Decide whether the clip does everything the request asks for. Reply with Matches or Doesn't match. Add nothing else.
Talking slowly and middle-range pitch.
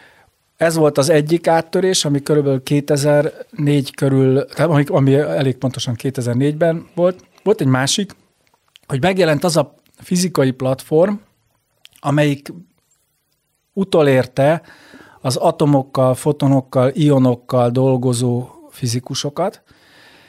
Matches